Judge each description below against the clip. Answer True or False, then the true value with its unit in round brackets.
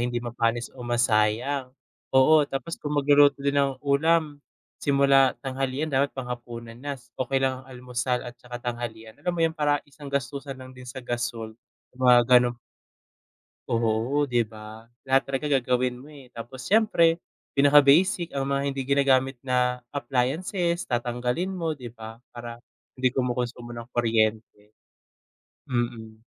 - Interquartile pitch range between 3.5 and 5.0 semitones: False (2.6 semitones)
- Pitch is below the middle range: True (130 Hz)